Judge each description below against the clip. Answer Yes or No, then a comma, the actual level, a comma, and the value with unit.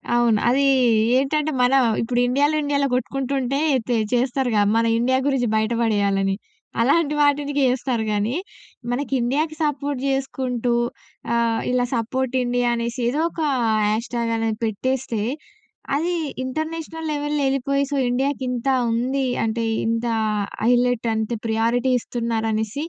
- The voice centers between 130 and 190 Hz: No, very high, 250 Hz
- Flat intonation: No, average, 3.2 semitones